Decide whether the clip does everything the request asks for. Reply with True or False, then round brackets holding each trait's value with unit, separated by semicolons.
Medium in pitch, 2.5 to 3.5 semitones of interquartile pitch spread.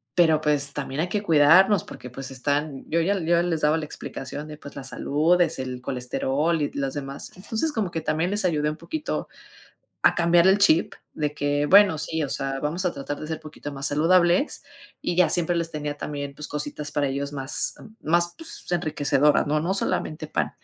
True (155 Hz; 3.2 semitones)